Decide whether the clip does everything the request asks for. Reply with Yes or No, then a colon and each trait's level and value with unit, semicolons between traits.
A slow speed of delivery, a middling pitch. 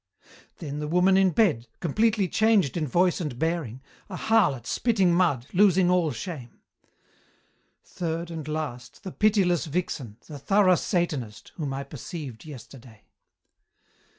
Yes: slow, 130 wpm; medium, 165 Hz